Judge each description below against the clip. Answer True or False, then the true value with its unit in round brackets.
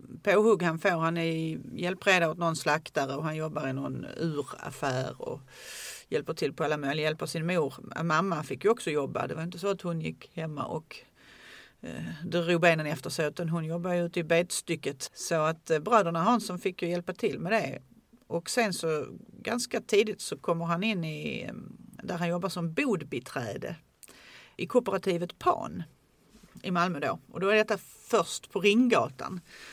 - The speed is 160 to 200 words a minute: True (180 wpm)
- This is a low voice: False (175 Hz)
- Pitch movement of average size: True (4.1 semitones)